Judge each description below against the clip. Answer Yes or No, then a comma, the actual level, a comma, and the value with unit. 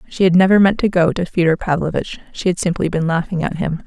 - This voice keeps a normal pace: No, fast, 250 wpm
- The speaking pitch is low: No, medium, 175 Hz